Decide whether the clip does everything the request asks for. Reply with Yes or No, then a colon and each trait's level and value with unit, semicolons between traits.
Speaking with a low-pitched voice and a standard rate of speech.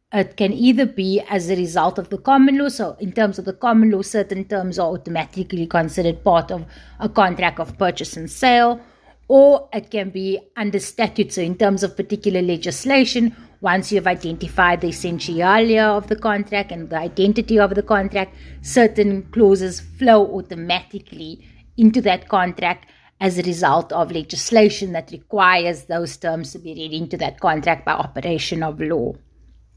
No: high, 190 Hz; average, 170 wpm